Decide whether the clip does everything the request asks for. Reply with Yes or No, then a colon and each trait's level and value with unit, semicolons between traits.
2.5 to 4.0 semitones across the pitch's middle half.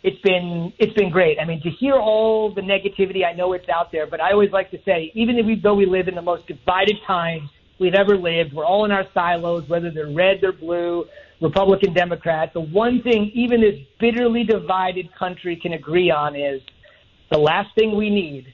Yes: average, 3.3 semitones